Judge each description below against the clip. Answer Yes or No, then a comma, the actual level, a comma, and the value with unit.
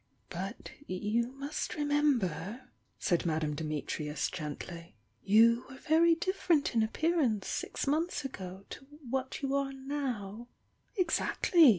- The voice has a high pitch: Yes, high, 245 Hz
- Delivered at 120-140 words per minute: Yes, slow, 135 wpm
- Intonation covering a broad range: Yes, wide, 7.8 semitones